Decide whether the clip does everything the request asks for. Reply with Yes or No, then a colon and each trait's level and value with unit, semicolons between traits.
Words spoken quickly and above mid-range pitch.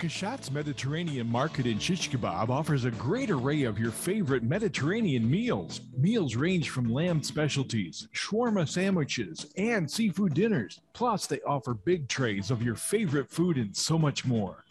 No: fast, 150 wpm; medium, 145 Hz